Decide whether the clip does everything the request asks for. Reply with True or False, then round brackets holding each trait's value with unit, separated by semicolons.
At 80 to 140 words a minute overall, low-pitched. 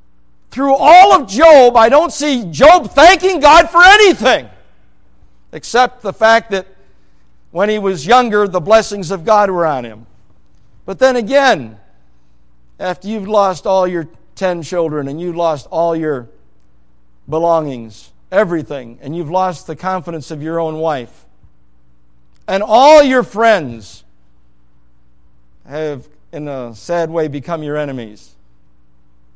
False (135 wpm; 160 Hz)